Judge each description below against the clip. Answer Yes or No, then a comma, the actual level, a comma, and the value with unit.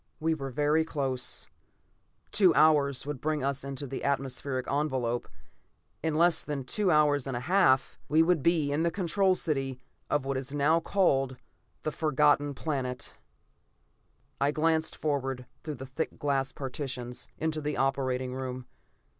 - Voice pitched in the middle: Yes, medium, 145 Hz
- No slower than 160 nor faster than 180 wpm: No, average, 150 wpm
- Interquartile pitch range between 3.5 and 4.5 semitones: No, average, 2.9 semitones